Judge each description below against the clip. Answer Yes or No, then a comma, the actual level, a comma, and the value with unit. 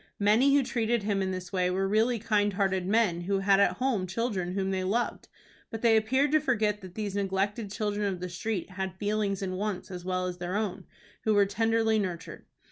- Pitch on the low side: No, high, 200 Hz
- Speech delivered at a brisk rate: Yes, fast, 210 wpm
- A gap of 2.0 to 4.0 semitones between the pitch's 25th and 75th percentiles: Yes, average, 2.8 semitones